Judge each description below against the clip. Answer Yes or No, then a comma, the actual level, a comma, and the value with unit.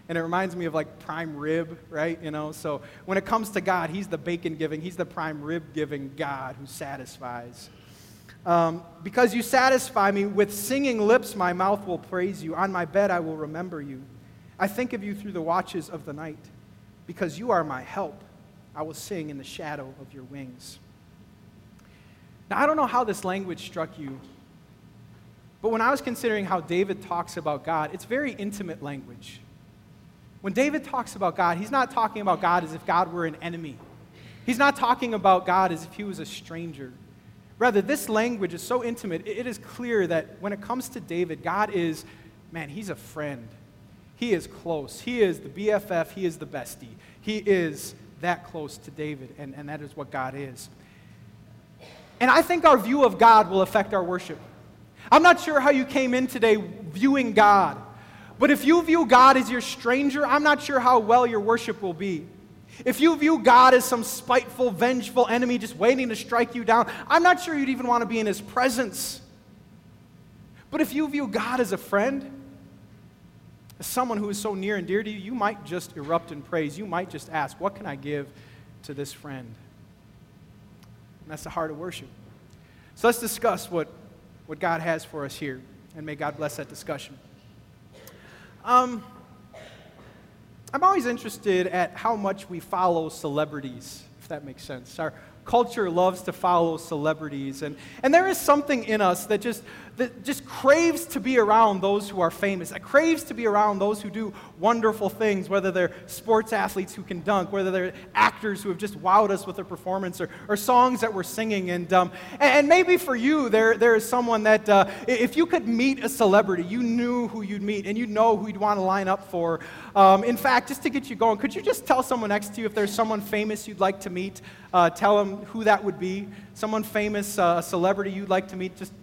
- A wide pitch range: Yes, wide, 6.2 semitones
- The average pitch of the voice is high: Yes, high, 195 Hz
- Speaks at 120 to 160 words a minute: No, fast, 205 wpm